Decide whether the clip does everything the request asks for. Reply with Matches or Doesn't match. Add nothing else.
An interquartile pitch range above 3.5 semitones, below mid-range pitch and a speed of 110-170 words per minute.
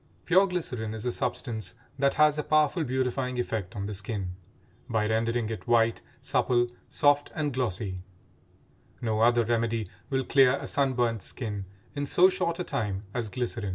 Matches